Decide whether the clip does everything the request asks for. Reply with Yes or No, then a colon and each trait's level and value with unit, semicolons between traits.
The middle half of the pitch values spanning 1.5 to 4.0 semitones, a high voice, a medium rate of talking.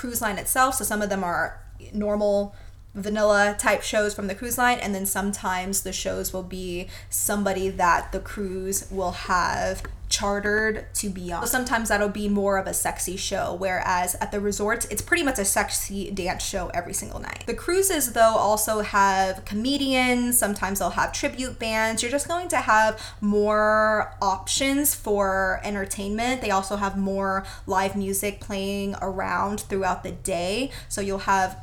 Yes: narrow, 2.4 semitones; high, 205 Hz; average, 170 wpm